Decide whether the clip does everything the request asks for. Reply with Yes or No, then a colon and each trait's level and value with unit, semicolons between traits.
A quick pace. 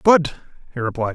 No: average, 155 wpm